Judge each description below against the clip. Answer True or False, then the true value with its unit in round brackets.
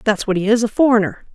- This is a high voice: True (220 Hz)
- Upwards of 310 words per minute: False (225 wpm)